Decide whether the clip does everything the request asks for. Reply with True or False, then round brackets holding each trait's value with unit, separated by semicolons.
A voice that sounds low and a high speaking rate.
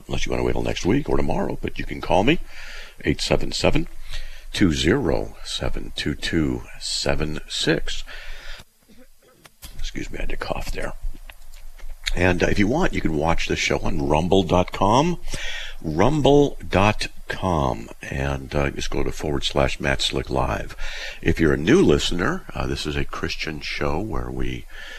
False (70 Hz; 145 wpm)